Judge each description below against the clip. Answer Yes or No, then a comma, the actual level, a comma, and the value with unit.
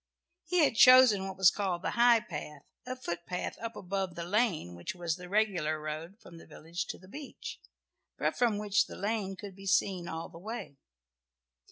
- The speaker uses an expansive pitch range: No, average, 4.1 semitones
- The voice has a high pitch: Yes, high, 195 Hz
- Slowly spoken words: No, average, 190 wpm